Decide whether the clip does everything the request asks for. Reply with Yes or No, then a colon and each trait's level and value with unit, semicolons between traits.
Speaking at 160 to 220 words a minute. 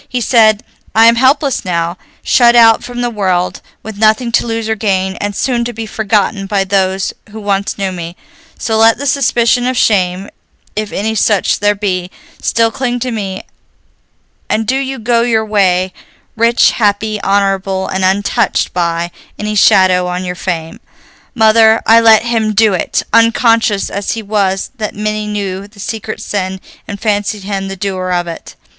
Yes: average, 175 wpm